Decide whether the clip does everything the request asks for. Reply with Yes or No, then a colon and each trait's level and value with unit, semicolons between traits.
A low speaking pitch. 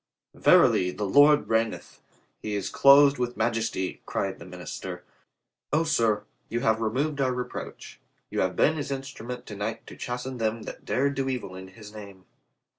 Yes: low, 115 Hz